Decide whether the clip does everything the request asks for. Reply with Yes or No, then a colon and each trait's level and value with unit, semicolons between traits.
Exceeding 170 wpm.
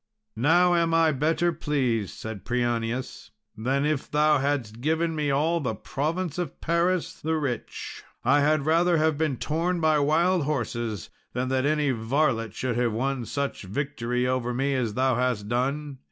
No: average, 165 wpm